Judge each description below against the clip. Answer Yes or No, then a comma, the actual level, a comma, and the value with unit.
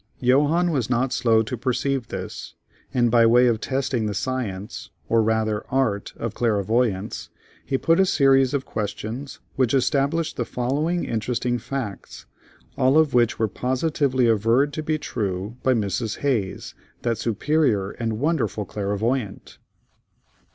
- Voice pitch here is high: No, low, 120 Hz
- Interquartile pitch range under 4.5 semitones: Yes, average, 3.7 semitones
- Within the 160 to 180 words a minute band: No, average, 140 wpm